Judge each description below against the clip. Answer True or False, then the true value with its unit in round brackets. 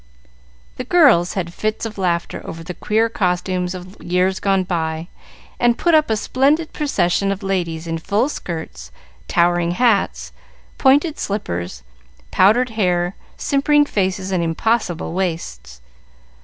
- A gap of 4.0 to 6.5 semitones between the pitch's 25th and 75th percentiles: True (4.8 semitones)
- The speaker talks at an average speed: False (130 wpm)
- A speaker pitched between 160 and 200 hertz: True (185 Hz)